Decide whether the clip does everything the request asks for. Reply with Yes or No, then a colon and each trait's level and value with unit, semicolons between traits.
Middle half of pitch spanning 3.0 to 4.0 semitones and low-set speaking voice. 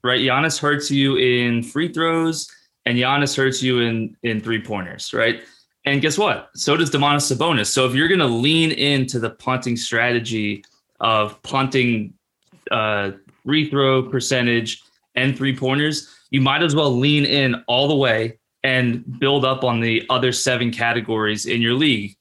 Yes: average, 3.3 semitones; low, 130 Hz